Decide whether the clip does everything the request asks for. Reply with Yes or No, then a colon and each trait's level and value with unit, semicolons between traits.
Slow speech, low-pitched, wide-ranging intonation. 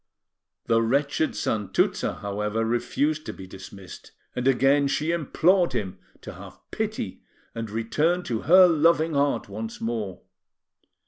Yes: slow, 130 wpm; low, 120 Hz; wide, 6.1 semitones